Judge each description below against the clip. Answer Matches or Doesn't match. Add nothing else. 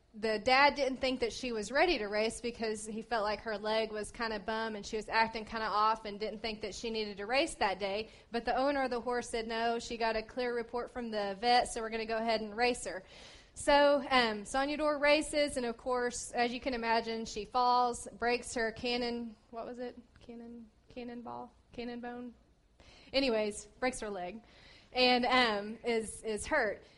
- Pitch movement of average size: Doesn't match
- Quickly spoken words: Matches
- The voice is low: Doesn't match